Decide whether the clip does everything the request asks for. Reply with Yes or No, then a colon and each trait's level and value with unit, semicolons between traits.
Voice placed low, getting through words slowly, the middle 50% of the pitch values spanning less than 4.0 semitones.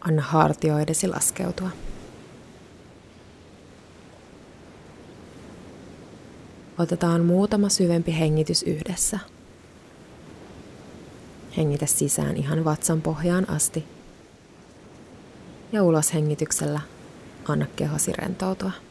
No: medium, 160 Hz; slow, 65 wpm; average, 2.9 semitones